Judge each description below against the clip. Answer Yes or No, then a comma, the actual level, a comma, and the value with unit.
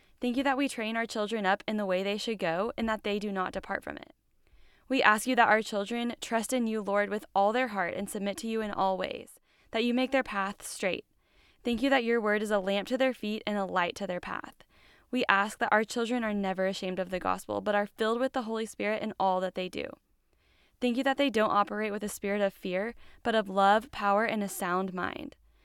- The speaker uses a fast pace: Yes, fast, 255 wpm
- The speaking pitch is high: Yes, high, 210 Hz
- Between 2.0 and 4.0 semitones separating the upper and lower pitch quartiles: Yes, average, 2.9 semitones